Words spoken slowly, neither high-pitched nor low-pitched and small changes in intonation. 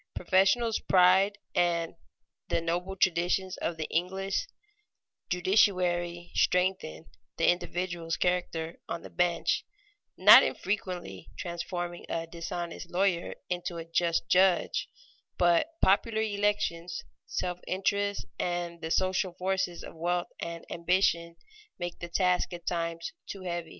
Yes: slow, 120 wpm; medium, 175 Hz; narrow, 1.8 semitones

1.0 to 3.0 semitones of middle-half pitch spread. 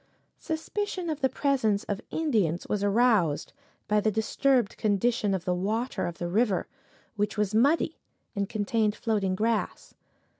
No: average, 3.8 semitones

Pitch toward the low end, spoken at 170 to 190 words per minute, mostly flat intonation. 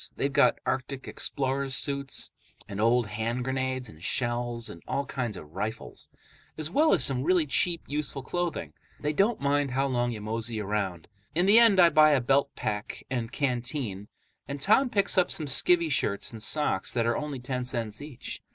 No: low, 130 Hz; average, 185 wpm; average, 4.4 semitones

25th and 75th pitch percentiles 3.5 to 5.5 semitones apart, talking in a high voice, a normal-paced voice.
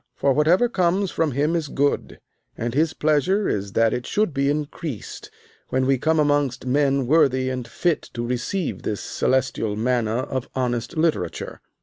No: average, 4.2 semitones; medium, 140 Hz; average, 160 wpm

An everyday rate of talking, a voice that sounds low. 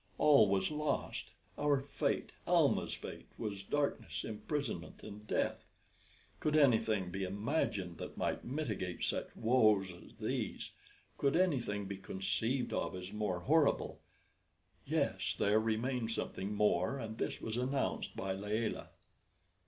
No: slow, 130 wpm; low, 110 Hz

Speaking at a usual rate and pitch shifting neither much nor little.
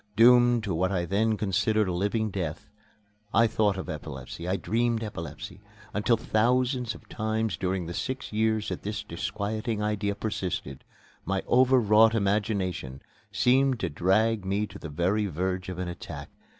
Yes: average, 160 wpm; average, 3.4 semitones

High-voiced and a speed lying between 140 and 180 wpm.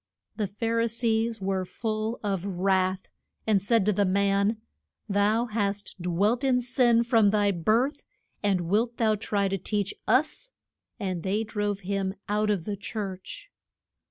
Yes: high, 205 Hz; average, 155 wpm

